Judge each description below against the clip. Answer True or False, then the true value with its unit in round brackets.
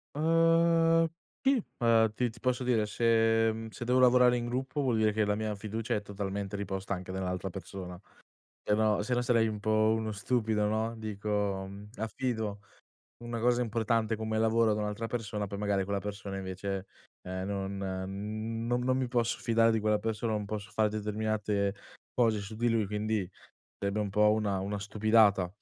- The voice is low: True (110 Hz)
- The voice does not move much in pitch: True (2.1 semitones)